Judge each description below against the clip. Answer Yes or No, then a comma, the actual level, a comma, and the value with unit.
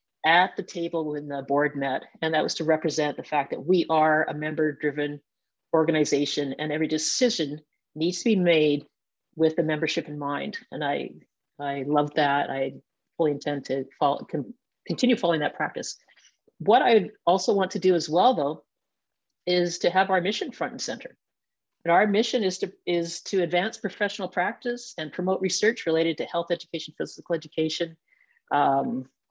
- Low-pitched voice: No, medium, 165 Hz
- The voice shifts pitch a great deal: No, average, 3.8 semitones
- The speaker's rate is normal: Yes, average, 170 wpm